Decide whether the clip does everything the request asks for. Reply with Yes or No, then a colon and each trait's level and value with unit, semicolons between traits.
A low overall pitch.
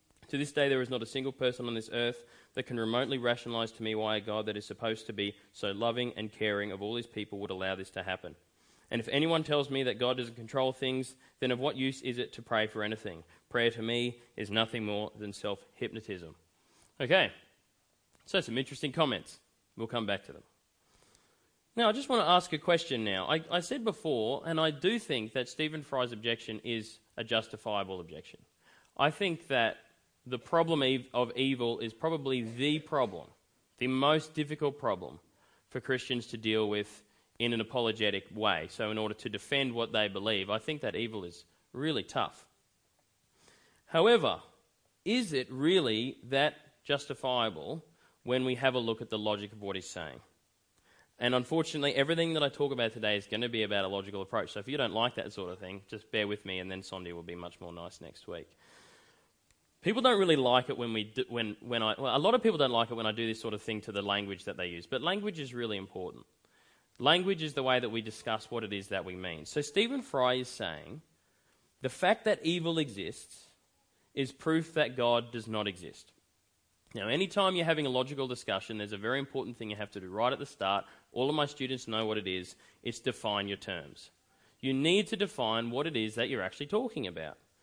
Yes: low, 120 Hz